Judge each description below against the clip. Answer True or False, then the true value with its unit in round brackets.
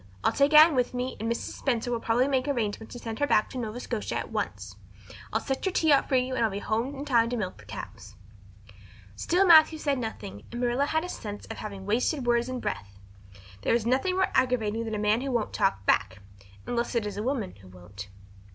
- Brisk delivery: True (235 wpm)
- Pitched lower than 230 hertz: False (240 Hz)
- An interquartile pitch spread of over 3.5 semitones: True (4.0 semitones)